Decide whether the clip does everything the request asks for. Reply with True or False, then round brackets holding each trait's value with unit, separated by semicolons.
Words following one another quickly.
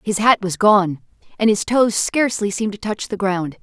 True (215 wpm)